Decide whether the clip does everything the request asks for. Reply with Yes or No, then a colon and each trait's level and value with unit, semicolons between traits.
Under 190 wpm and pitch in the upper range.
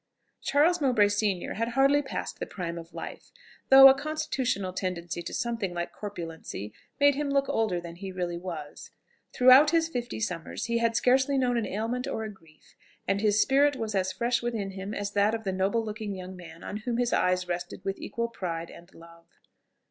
No: average, 195 wpm; high, 210 Hz